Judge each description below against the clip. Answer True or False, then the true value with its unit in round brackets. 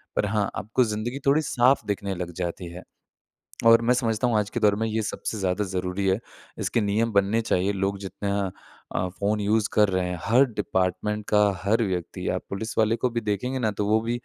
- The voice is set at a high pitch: False (105 Hz)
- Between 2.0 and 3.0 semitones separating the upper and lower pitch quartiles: True (2.6 semitones)